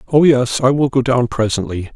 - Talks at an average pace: No, fast, 215 wpm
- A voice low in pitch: Yes, low, 125 Hz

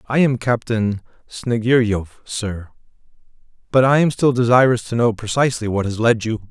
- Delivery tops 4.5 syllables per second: Yes, 4.9 syllables/s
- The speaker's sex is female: No, male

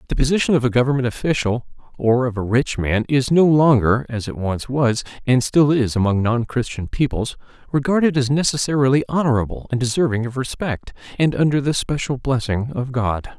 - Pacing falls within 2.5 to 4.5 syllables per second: No, 5.5 syllables/s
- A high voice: No, low, 130 Hz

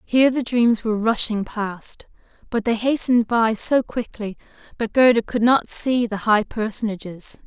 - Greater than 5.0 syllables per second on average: No, 4.6 syllables/s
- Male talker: No, female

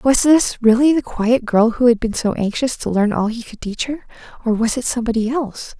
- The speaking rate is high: Yes, fast, 240 wpm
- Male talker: No, female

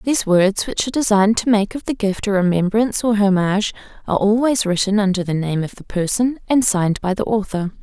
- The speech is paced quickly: Yes, fast, 215 wpm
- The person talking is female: Yes, female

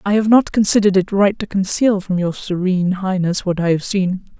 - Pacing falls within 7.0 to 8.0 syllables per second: No, 5.5 syllables/s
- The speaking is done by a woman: Yes, female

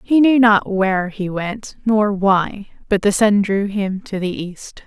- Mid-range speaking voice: No, high, 200 Hz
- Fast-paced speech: No, average, 195 wpm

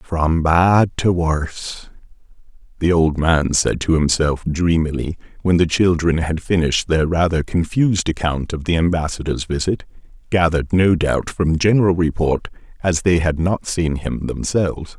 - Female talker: No, male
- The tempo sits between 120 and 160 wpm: Yes, average, 150 wpm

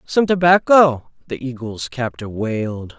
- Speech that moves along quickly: No, slow, 120 wpm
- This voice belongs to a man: Yes, male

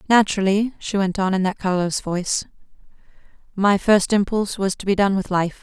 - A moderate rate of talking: Yes, average, 180 wpm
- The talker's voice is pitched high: Yes, high, 195 Hz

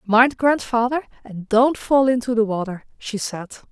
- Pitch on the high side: Yes, high, 235 Hz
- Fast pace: No, average, 160 wpm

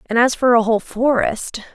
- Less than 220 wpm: Yes, fast, 205 wpm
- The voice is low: No, high, 235 Hz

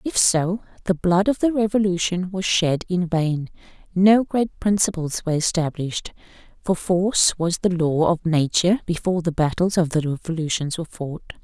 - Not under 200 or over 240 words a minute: No, average, 165 wpm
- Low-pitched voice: No, medium, 175 Hz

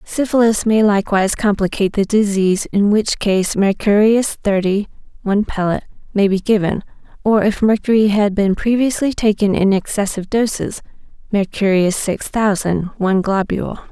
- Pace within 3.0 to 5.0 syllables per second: No, 5.2 syllables/s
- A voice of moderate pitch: No, high, 205 Hz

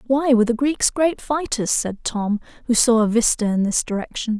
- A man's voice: No, female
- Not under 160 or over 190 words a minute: No, fast, 205 wpm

